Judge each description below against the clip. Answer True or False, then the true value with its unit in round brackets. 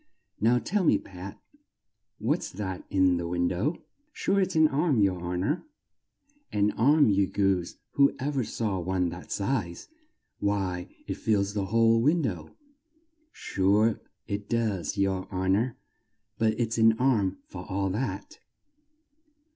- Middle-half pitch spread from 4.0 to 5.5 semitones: True (4.6 semitones)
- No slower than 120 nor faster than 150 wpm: True (145 wpm)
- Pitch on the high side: False (100 Hz)